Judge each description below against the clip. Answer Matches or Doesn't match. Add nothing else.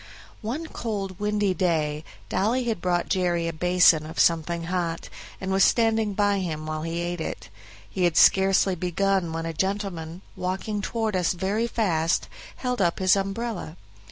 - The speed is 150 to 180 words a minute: Matches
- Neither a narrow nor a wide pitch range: Matches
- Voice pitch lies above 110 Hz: Matches